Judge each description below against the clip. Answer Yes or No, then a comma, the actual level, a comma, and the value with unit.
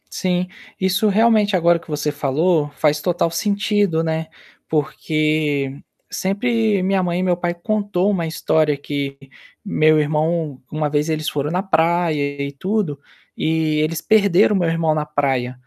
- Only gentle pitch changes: No, average, 3.8 semitones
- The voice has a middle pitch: Yes, medium, 165 Hz